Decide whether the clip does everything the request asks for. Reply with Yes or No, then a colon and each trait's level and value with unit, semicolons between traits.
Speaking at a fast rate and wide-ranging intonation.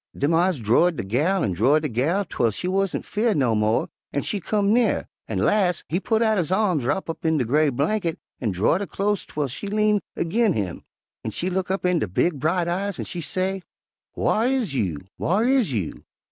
Yes: fast, 215 wpm; wide, 6.5 semitones